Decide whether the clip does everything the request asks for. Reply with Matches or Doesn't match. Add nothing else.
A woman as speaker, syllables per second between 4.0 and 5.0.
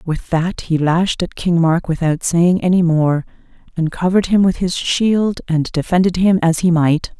Matches